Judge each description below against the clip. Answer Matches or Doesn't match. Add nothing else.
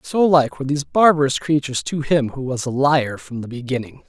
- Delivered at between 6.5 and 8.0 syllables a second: Doesn't match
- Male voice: Matches